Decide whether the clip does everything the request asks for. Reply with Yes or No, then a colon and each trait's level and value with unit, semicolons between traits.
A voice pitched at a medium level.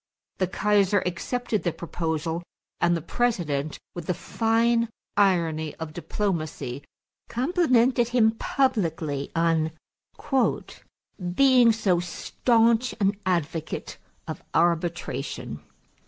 Yes: medium, 180 Hz